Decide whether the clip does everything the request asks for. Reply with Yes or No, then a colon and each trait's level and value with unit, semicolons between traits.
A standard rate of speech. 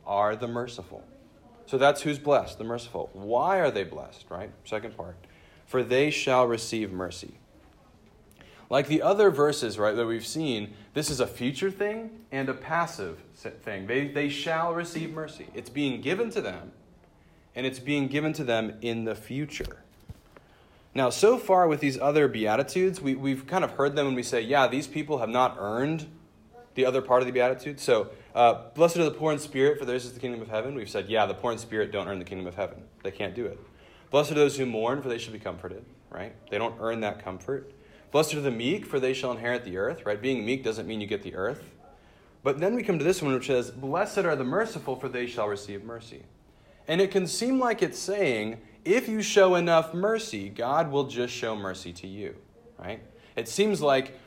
No: fast, 215 wpm